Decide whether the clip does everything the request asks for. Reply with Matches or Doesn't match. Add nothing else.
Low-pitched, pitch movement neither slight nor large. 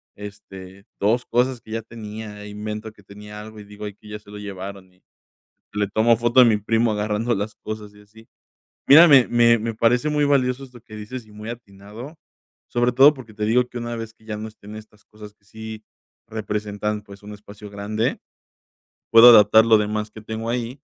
Doesn't match